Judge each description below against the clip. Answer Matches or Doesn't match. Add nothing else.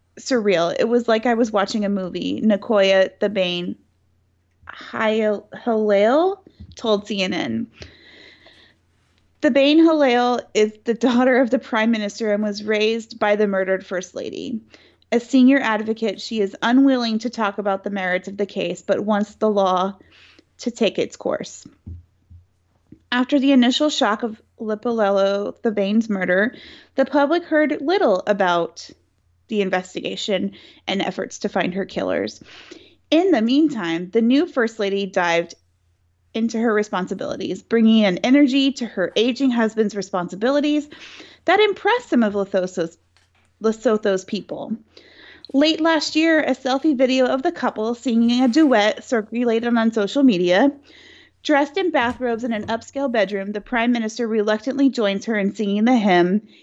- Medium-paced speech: Matches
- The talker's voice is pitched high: Matches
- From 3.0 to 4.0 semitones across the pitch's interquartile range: Doesn't match